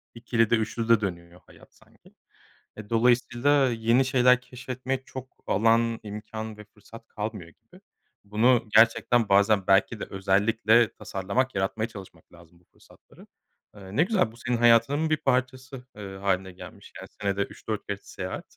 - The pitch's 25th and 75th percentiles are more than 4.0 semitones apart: No, average, 3.7 semitones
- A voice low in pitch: Yes, low, 110 Hz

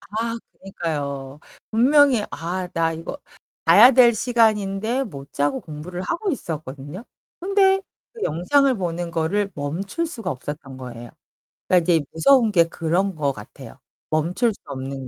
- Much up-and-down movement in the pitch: Yes, wide, 7.6 semitones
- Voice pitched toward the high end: No, medium, 180 Hz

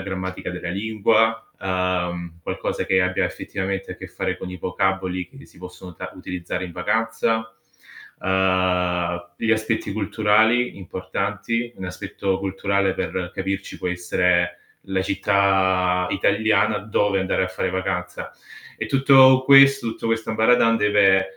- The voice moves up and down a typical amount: Yes, average, 3.1 semitones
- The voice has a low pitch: Yes, very low, 95 Hz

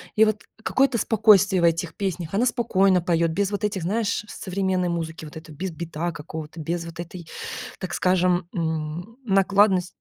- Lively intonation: No, average, 3.1 semitones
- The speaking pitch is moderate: Yes, medium, 180 Hz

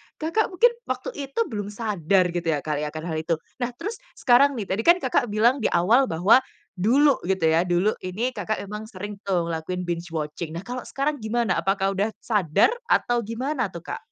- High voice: Yes, high, 205 Hz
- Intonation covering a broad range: Yes, wide, 5.8 semitones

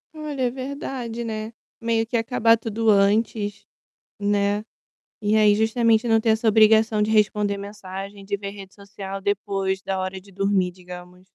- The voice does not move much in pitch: Yes, narrow, 2.3 semitones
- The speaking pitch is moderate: No, high, 210 Hz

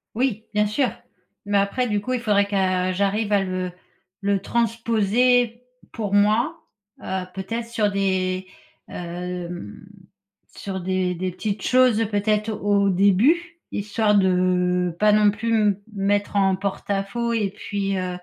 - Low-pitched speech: No, high, 200 Hz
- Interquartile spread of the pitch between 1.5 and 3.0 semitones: Yes, average, 2.7 semitones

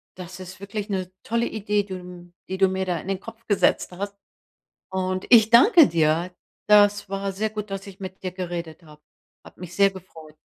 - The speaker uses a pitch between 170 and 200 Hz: Yes, high, 190 Hz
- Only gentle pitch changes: Yes, narrow, 2.2 semitones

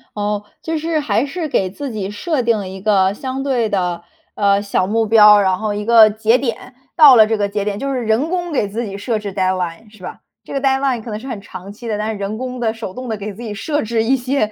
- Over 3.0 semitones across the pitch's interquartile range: Yes, average, 3.9 semitones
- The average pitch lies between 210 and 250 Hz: Yes, high, 220 Hz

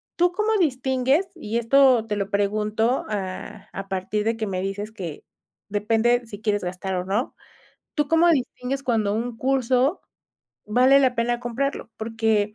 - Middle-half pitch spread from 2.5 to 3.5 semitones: No, average, 3.9 semitones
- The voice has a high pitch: Yes, high, 225 Hz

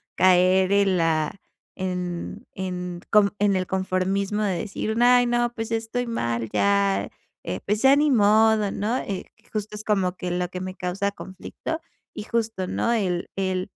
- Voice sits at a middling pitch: No, high, 195 Hz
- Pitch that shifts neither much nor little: Yes, average, 3.2 semitones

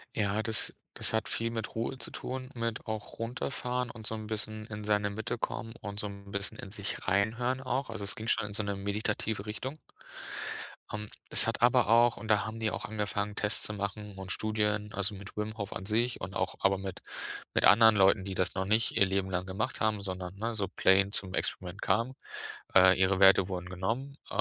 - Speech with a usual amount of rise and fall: No, narrow, 2.3 semitones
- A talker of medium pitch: No, low, 105 Hz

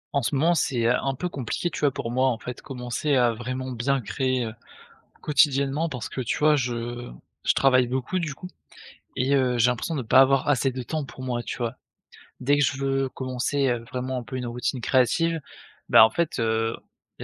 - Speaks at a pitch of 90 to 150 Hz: Yes, low, 130 Hz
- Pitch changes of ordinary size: No, narrow, 2.3 semitones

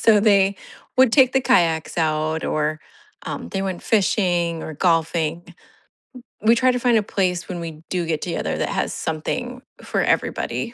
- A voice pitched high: No, medium, 180 Hz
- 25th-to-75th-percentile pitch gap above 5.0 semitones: Yes, wide, 5.4 semitones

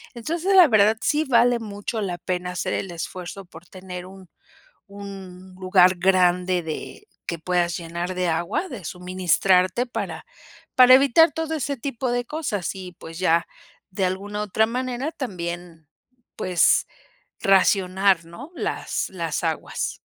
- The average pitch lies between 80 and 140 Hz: No, high, 190 Hz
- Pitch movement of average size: Yes, average, 4.9 semitones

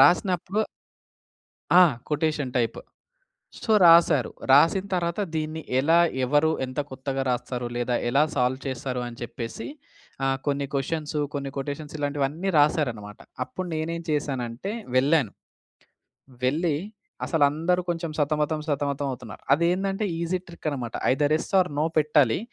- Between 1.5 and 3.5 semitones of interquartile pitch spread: No, average, 3.9 semitones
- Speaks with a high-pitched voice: No, medium, 145 Hz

